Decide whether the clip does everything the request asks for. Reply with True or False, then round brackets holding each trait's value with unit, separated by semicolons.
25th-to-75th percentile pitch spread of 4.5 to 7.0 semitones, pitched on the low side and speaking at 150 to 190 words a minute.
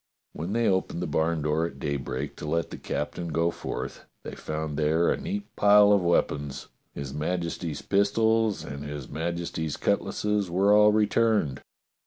True (5.4 semitones; 85 Hz; 165 wpm)